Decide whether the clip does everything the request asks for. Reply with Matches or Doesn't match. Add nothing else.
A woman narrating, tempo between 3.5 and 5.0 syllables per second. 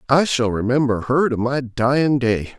Doesn't match